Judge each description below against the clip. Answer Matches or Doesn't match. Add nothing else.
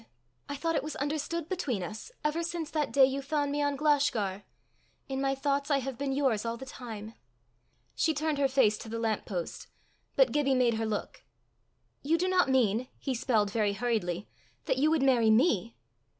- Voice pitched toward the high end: Matches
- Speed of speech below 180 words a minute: Doesn't match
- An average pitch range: Matches